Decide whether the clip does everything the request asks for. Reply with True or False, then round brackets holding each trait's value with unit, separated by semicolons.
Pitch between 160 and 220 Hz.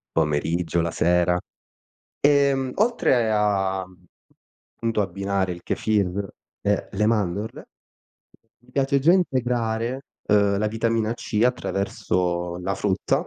False (105 Hz)